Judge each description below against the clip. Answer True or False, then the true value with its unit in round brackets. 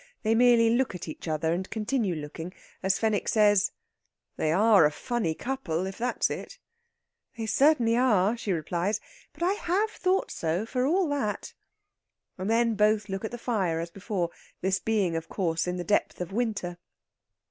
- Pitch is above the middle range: True (210 Hz)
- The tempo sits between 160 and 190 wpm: True (175 wpm)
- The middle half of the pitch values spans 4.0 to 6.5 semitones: True (5.0 semitones)